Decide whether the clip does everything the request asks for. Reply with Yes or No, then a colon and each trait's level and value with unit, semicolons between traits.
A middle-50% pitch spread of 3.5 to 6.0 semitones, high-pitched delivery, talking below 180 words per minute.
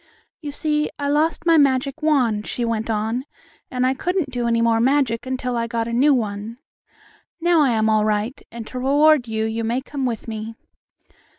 No: average, 4.0 semitones; very high, 250 Hz; average, 195 wpm